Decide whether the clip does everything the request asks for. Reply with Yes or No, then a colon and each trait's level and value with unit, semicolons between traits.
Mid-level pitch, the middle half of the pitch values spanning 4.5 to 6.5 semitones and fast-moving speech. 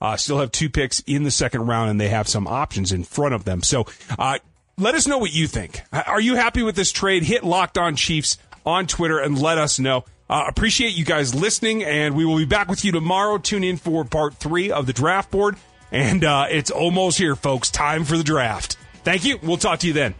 Yes: medium, 160 Hz; wide, 5.4 semitones; fast, 240 wpm